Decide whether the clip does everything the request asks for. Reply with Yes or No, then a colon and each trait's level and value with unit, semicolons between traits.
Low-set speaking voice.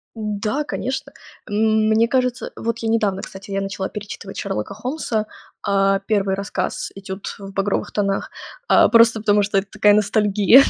No: high, 210 Hz